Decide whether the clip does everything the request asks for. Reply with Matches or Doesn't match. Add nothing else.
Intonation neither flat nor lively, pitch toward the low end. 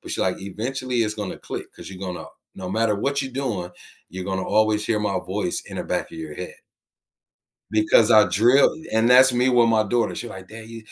Matches